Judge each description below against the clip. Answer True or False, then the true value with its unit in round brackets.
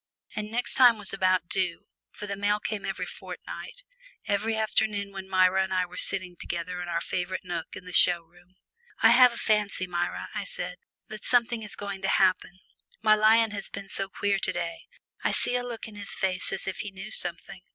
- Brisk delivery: True (210 wpm)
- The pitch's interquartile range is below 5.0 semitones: True (2.7 semitones)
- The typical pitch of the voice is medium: False (195 Hz)